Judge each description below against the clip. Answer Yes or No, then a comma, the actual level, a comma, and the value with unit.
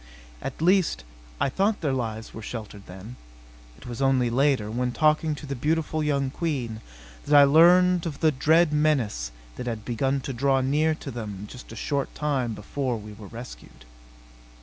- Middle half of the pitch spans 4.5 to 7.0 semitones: Yes, average, 4.8 semitones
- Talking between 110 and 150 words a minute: No, average, 175 wpm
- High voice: No, low, 135 Hz